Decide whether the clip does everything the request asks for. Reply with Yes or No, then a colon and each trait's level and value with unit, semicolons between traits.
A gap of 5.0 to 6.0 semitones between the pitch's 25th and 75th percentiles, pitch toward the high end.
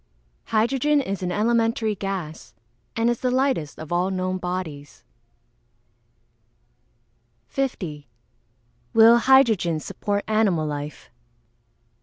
Yes: average, 5.3 semitones; high, 200 Hz